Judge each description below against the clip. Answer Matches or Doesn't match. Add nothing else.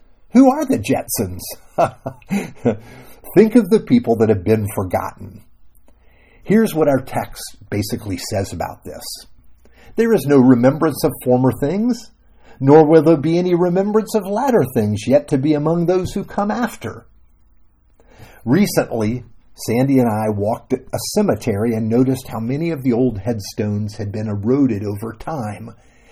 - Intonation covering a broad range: Matches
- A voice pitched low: Matches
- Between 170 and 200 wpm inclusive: Doesn't match